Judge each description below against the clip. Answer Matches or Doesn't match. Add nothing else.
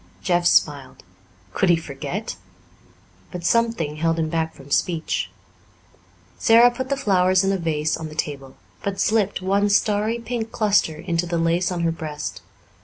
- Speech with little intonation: Doesn't match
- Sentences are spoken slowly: Doesn't match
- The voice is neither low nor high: Matches